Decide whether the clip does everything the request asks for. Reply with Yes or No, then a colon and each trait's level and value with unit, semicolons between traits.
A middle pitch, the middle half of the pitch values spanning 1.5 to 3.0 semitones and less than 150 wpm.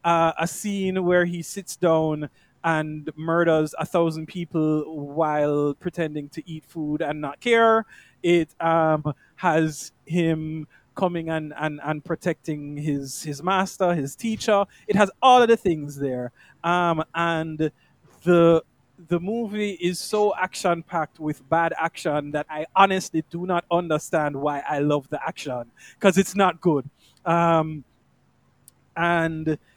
Yes: medium, 160 Hz; average, 2.7 semitones; average, 140 wpm